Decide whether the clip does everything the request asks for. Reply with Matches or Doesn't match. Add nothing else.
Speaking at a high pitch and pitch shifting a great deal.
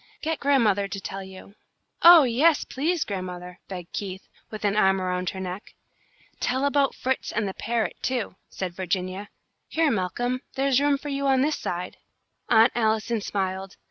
Matches